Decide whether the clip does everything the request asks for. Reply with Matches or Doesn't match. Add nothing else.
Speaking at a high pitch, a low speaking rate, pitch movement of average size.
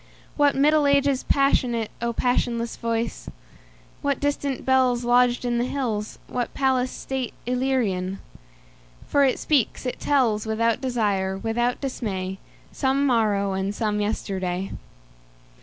Matches